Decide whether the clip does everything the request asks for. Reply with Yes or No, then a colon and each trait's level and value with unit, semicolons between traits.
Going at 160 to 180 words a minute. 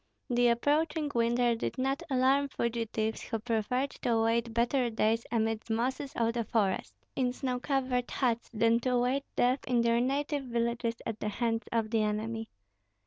Yes: average, 165 wpm